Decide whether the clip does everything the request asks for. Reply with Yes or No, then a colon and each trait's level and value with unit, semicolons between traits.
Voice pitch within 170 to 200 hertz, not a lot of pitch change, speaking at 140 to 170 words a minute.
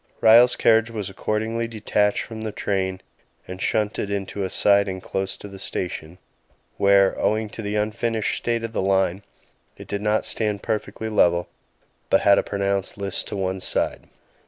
No: low, 100 Hz; narrow, 2.2 semitones; average, 165 wpm